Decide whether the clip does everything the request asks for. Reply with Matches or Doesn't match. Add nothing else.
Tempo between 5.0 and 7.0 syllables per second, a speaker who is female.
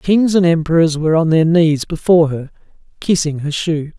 Doesn't match